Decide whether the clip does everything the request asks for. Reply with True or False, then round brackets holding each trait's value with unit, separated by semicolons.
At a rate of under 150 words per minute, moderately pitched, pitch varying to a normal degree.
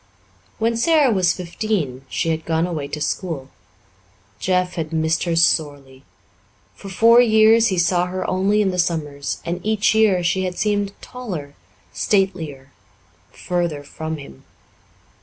True (140 wpm; 180 Hz; 4.3 semitones)